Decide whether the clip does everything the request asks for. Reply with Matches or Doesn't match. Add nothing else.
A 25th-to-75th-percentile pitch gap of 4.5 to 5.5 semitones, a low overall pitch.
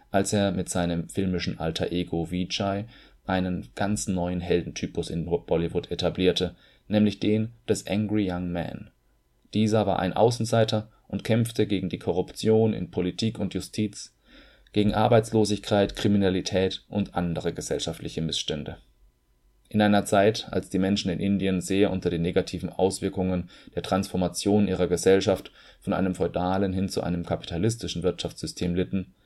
Doesn't match